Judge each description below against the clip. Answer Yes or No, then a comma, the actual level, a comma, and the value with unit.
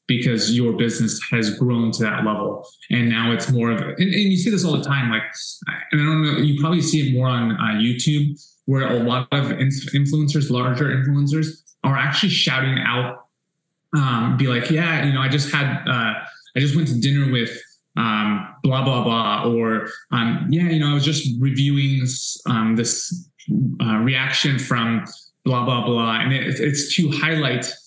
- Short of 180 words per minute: No, average, 190 wpm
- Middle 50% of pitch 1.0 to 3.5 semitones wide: No, average, 4.0 semitones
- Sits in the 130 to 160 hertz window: Yes, low, 135 Hz